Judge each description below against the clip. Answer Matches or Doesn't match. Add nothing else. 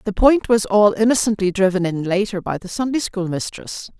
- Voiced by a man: Doesn't match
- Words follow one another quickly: Doesn't match